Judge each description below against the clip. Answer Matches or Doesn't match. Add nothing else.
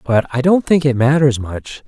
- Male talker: Matches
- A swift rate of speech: Matches